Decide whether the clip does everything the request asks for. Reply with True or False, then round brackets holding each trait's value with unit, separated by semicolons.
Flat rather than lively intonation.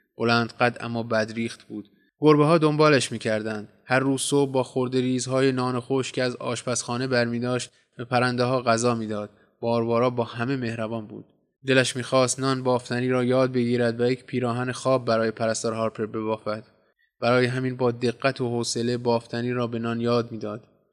True (1.8 semitones)